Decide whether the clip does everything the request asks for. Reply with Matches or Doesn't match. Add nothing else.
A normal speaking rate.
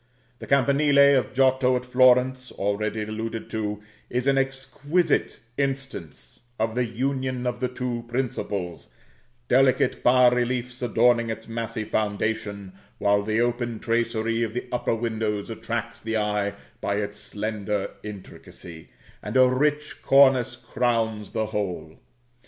Doesn't match